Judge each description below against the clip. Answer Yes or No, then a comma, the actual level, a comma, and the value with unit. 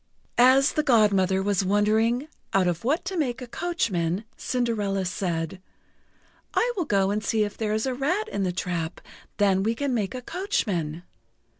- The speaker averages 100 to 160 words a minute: No, average, 170 wpm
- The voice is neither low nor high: No, high, 210 Hz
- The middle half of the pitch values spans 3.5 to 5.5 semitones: Yes, average, 5.1 semitones